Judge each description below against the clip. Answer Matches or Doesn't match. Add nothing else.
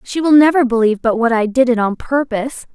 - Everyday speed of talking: Doesn't match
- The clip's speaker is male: Doesn't match